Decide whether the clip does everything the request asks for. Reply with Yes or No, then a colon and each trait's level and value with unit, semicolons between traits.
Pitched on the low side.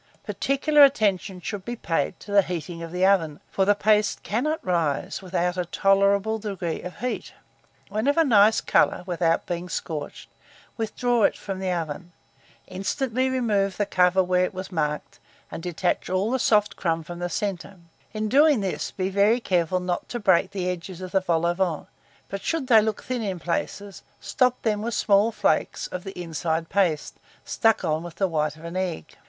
No: high, 190 Hz